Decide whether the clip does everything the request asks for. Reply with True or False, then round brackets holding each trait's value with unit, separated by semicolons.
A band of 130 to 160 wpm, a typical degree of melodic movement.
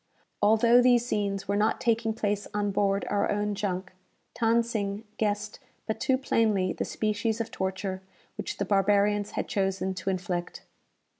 False (155 wpm; 2.1 semitones)